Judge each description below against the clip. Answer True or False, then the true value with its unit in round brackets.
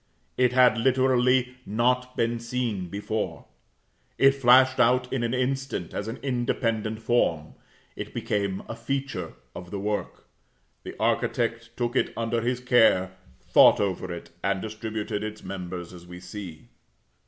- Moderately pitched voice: False (115 Hz)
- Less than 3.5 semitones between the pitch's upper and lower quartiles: False (4.0 semitones)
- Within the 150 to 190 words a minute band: False (140 wpm)